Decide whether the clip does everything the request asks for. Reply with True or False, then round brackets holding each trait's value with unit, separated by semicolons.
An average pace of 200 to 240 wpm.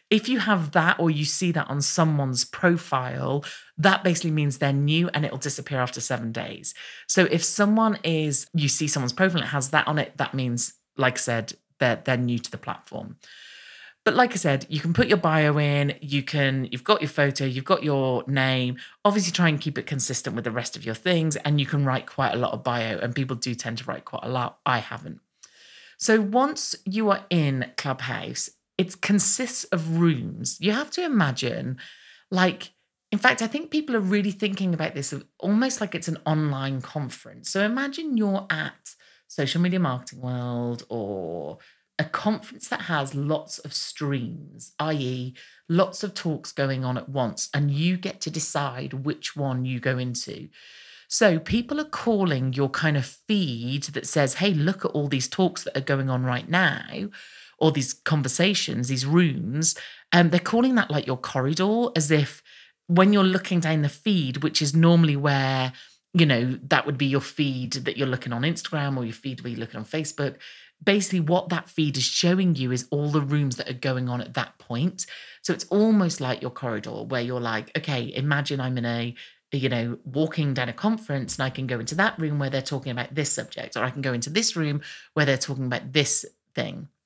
True (205 wpm)